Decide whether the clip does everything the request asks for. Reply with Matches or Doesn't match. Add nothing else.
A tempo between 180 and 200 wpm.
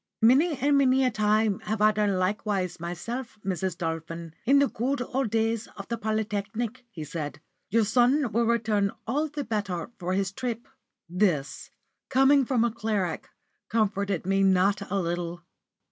Doesn't match